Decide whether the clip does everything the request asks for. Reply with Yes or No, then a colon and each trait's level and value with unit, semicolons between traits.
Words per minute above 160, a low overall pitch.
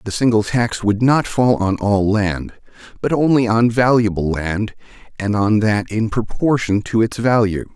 Yes: average, 170 wpm; low, 110 Hz